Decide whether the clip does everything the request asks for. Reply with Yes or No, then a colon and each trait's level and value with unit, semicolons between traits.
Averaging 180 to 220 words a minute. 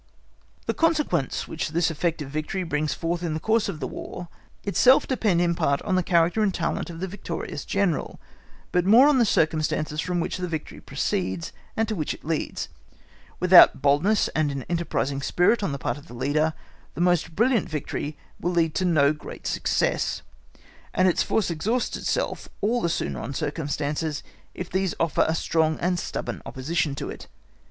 Yes: average, 185 wpm